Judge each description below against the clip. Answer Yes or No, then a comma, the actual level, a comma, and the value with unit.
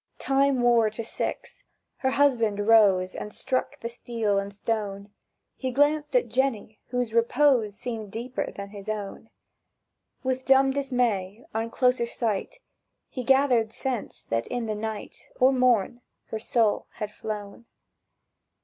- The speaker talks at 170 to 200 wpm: No, average, 140 wpm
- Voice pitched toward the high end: Yes, high, 230 Hz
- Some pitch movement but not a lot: Yes, average, 3.6 semitones